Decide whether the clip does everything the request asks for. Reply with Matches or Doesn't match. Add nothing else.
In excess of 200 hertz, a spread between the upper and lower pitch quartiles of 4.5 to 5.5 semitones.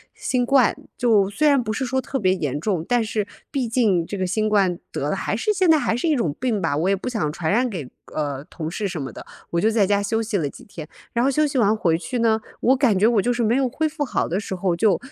Matches